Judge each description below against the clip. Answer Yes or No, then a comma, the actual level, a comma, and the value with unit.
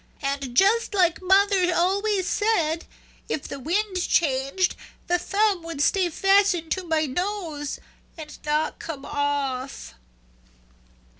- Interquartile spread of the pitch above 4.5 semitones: Yes, average, 4.9 semitones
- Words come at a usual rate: No, slow, 120 wpm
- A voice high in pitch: Yes, very high, 345 Hz